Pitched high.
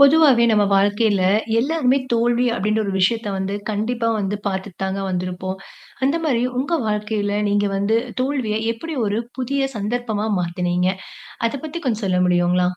Yes: high, 210 Hz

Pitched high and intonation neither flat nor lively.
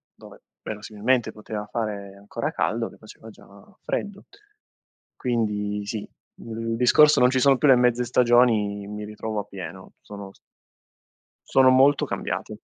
No: low, 110 Hz; average, 3.3 semitones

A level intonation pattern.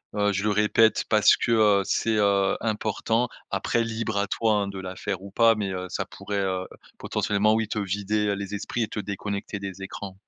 Yes: narrow, 1.6 semitones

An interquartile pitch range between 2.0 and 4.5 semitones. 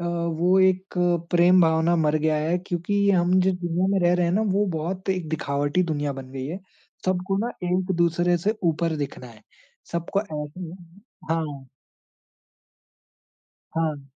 Yes: average, 2.9 semitones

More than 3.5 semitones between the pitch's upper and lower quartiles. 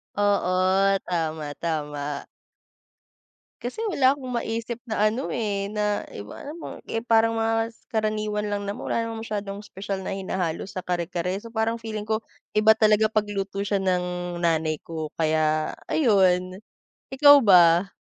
Yes: average, 3.9 semitones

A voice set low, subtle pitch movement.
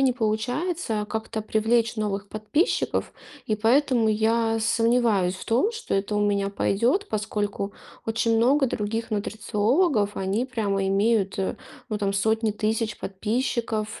No: high, 220 Hz; narrow, 2.2 semitones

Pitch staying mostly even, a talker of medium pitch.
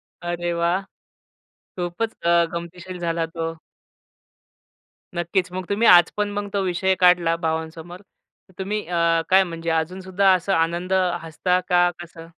Yes: narrow, 1.9 semitones; medium, 175 Hz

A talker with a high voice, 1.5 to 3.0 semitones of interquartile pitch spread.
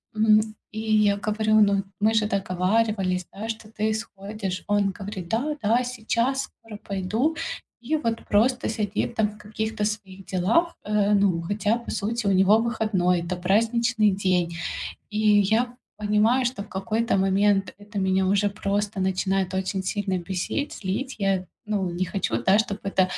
Yes: high, 205 Hz; narrow, 2.4 semitones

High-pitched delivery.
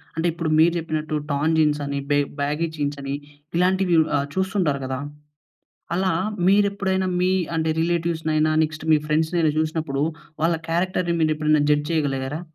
No: medium, 160 Hz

